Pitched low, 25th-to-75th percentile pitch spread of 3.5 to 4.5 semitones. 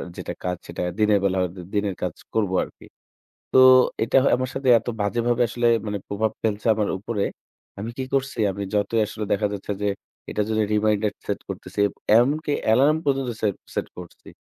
No: low, 105 Hz; average, 3.1 semitones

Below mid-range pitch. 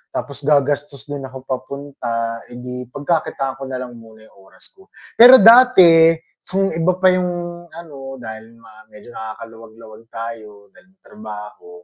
Yes: low, 130 Hz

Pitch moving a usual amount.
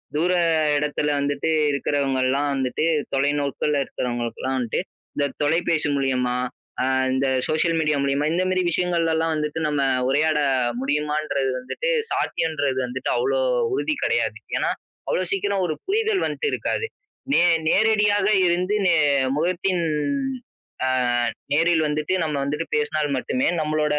Yes: average, 3.7 semitones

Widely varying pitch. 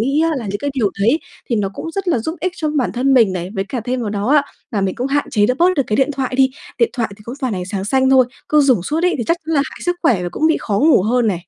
Yes: wide, 6.0 semitones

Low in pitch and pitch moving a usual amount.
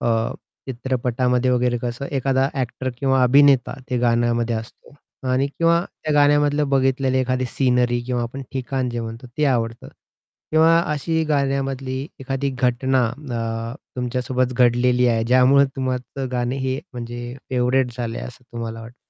No: low, 130 Hz; narrow, 1.8 semitones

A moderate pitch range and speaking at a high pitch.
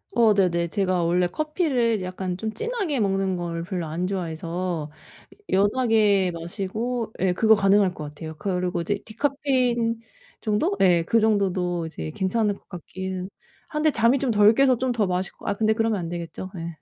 Yes: average, 4.3 semitones; high, 195 Hz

